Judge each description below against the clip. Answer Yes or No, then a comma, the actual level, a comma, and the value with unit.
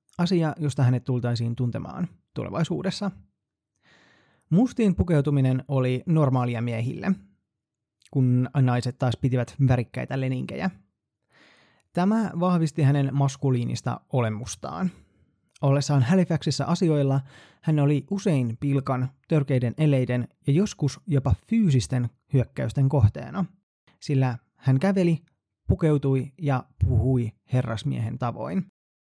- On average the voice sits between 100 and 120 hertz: No, low, 135 Hz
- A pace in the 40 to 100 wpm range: Yes, slow, 95 wpm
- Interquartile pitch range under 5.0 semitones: Yes, average, 4.6 semitones